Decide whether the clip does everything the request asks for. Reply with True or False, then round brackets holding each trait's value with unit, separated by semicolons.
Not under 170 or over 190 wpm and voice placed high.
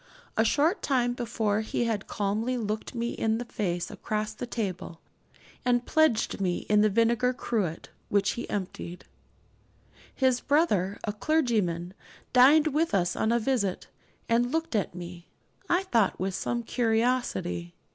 False (145 wpm; 225 Hz)